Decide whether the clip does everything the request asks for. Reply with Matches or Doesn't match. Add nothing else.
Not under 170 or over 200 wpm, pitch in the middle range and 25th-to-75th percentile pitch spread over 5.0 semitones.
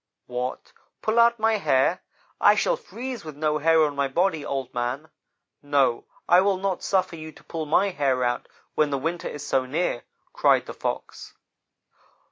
Matches